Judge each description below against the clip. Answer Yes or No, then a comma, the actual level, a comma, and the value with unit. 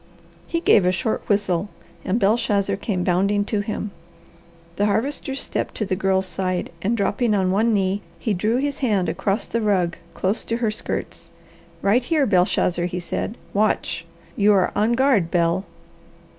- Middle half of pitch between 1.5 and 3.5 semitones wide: Yes, average, 3.1 semitones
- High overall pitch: Yes, high, 205 Hz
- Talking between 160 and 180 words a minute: Yes, average, 165 wpm